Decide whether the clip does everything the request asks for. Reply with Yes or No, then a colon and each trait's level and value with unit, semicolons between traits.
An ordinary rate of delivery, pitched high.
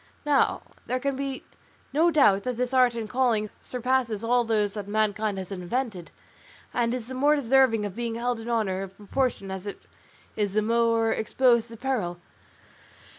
Yes: average, 175 wpm; high, 230 Hz